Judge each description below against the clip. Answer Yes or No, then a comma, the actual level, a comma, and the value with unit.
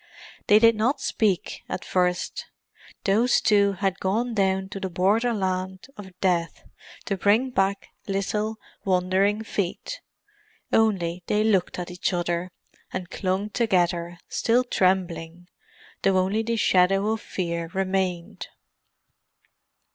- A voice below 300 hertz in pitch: Yes, high, 190 Hz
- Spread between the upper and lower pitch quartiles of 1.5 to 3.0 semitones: Yes, average, 2.7 semitones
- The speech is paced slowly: Yes, slow, 120 wpm